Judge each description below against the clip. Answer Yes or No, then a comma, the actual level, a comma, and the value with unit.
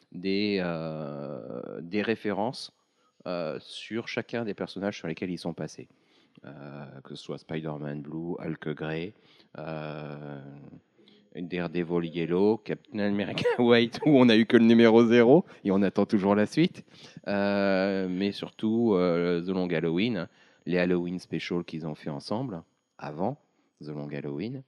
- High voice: No, very low, 90 Hz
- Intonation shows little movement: No, average, 4.8 semitones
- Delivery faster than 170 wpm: No, slow, 145 wpm